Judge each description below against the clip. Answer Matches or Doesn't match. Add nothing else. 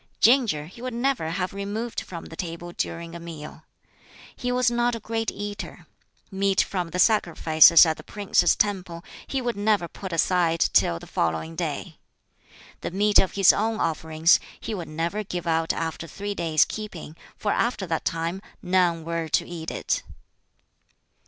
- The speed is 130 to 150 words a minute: Doesn't match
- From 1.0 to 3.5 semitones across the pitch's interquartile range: Doesn't match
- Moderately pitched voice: Matches